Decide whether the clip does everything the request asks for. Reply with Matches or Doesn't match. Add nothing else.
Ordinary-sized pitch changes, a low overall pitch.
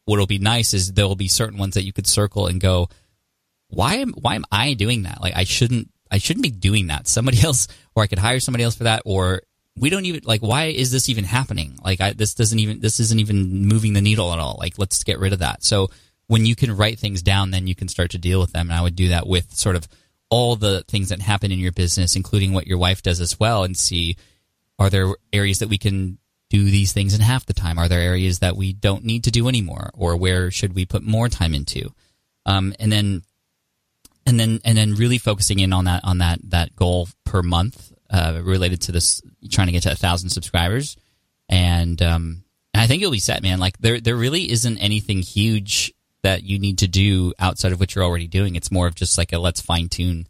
Matches